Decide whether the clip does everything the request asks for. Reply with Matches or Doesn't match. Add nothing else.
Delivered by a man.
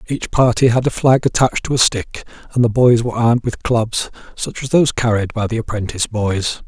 Matches